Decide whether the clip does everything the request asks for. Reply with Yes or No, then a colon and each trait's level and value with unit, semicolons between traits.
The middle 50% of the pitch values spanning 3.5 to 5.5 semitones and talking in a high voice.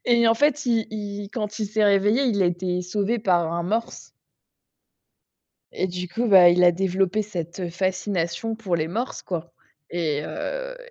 Yes: average, 4.1 semitones; high, 195 Hz